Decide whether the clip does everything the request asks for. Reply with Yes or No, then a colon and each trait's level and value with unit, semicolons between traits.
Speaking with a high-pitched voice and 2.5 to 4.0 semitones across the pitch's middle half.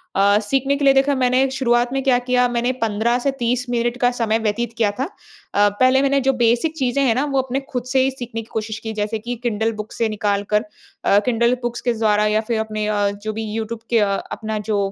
Yes: high, 235 Hz; average, 2.9 semitones